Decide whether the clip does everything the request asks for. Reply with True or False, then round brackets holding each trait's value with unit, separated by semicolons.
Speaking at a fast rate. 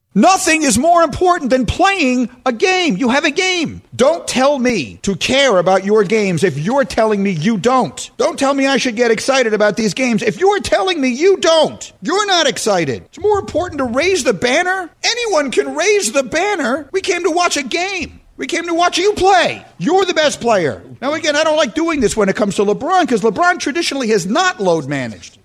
True (215 wpm)